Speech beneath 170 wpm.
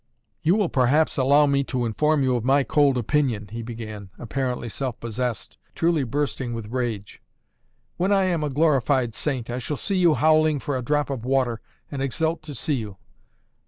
No: average, 185 wpm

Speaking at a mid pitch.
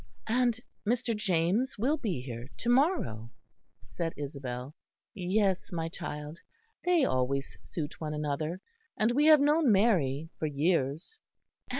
Yes: medium, 175 Hz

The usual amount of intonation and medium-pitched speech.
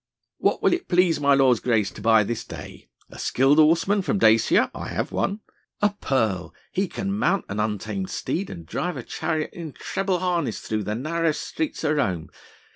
No: wide, 8.6 semitones; medium, 155 Hz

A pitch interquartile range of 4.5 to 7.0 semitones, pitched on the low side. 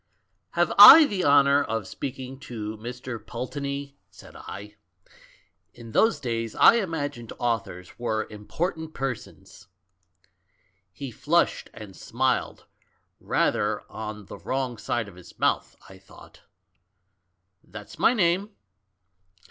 Yes: average, 4.9 semitones; low, 125 Hz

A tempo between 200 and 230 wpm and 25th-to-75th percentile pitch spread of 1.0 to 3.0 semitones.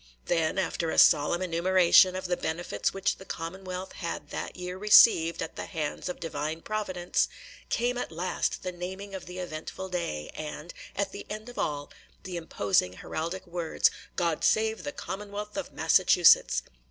No: average, 165 wpm; average, 2.7 semitones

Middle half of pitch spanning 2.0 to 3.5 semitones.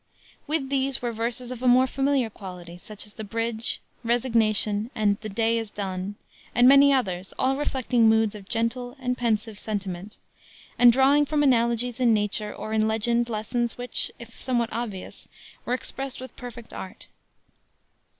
Yes: average, 2.7 semitones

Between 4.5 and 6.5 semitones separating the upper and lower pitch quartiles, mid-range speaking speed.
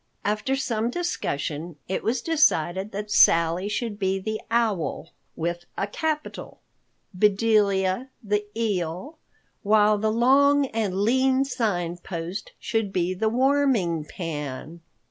No: average, 5.1 semitones; slow, 120 wpm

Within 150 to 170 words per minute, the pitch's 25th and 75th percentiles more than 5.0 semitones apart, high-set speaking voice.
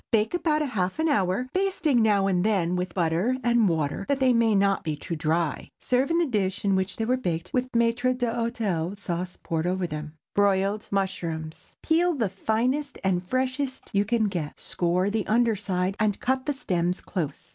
No: average, 190 wpm; wide, 5.6 semitones; high, 205 Hz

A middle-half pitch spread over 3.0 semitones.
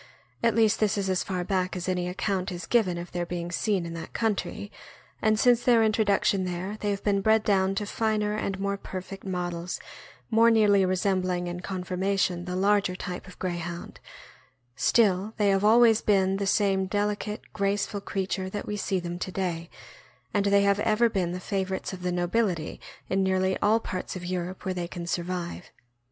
No: narrow, 2.4 semitones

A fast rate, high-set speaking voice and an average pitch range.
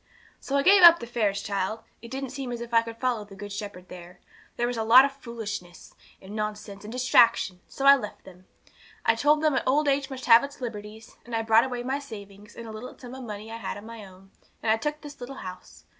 Yes: fast, 245 wpm; high, 230 Hz; average, 4.0 semitones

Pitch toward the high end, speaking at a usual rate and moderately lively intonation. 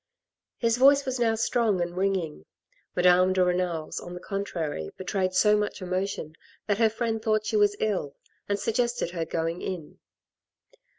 Yes: high, 195 Hz; average, 165 wpm; average, 3.7 semitones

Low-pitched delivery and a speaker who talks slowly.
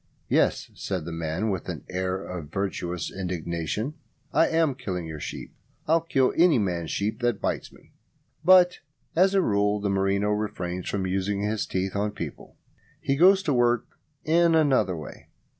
No: low, 100 Hz; average, 165 wpm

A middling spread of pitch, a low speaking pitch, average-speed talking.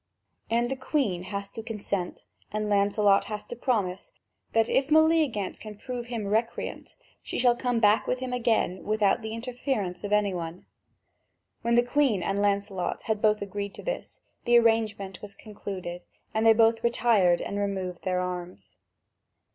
No: average, 3.1 semitones; high, 215 Hz; average, 165 wpm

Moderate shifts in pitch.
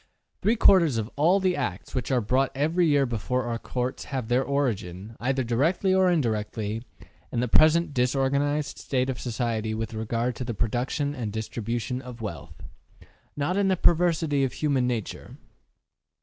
Yes: average, 4.1 semitones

